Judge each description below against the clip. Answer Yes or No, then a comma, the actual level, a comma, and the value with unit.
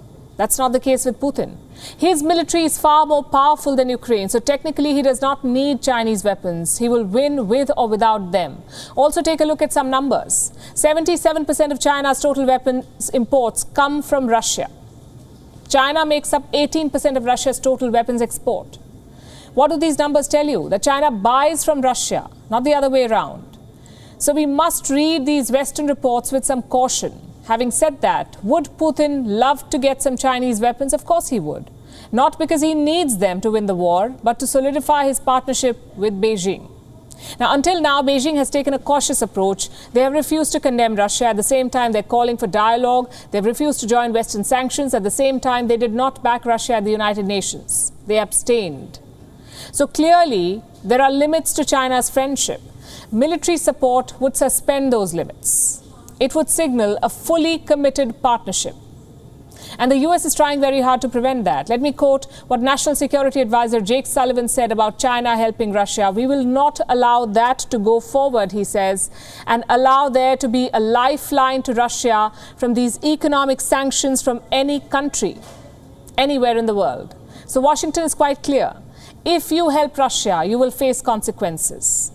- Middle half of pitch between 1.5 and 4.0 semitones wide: Yes, average, 3.6 semitones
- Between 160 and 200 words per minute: Yes, average, 175 wpm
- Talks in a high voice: Yes, very high, 260 Hz